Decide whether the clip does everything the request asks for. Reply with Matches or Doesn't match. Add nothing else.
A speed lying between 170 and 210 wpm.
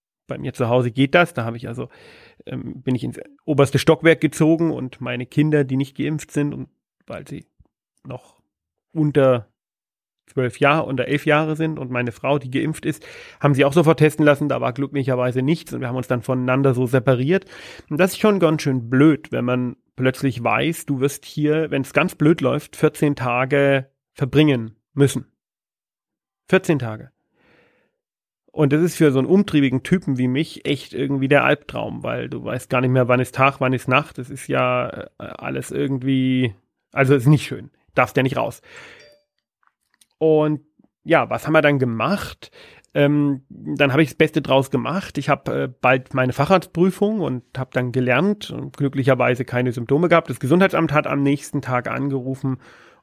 Matches